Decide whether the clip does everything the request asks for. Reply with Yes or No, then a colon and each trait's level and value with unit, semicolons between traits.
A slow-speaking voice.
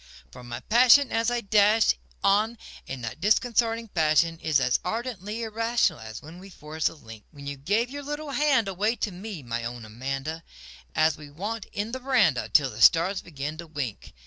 No: average, 190 wpm